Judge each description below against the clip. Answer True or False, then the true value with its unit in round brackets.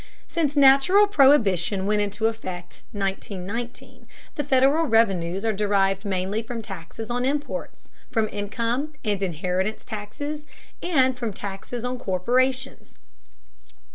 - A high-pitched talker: True (225 Hz)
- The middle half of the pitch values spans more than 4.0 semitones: True (5.2 semitones)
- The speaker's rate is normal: False (115 wpm)